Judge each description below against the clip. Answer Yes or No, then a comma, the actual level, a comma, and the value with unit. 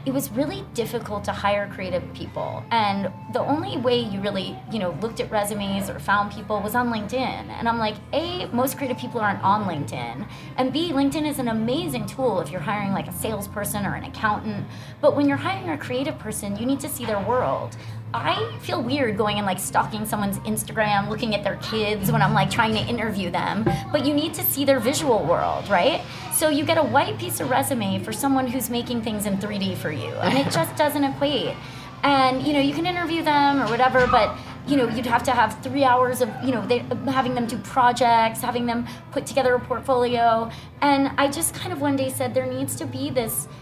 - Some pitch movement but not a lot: Yes, average, 4.5 semitones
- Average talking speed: No, fast, 220 wpm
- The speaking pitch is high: Yes, high, 245 Hz